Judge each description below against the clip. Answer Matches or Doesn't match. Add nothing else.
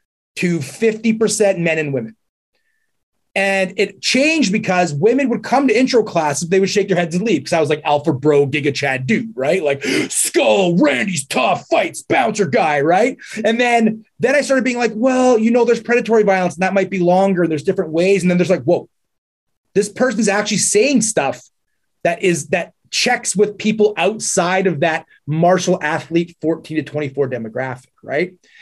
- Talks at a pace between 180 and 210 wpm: Matches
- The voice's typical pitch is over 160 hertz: Matches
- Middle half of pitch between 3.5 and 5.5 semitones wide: Matches